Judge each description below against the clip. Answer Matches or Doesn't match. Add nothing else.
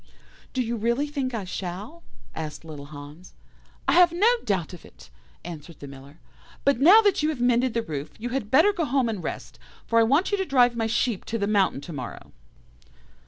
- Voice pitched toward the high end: Matches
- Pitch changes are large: Matches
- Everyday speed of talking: Doesn't match